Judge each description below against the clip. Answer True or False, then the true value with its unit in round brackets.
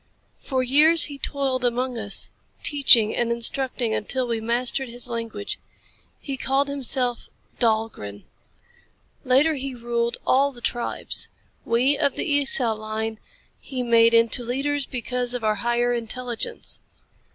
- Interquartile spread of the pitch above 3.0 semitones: False (2.6 semitones)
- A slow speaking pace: True (130 wpm)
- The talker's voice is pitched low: False (245 Hz)